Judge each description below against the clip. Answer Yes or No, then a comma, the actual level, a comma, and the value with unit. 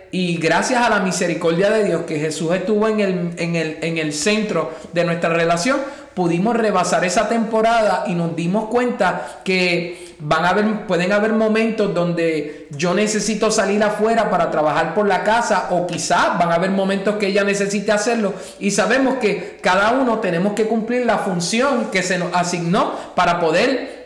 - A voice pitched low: No, high, 195 Hz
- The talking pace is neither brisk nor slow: Yes, average, 175 wpm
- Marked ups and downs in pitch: No, average, 4.0 semitones